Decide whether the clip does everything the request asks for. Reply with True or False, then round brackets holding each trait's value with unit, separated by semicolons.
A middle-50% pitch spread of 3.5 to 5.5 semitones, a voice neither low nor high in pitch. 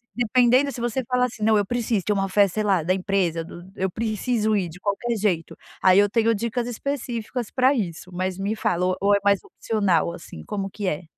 False (4.0 semitones; 205 Hz)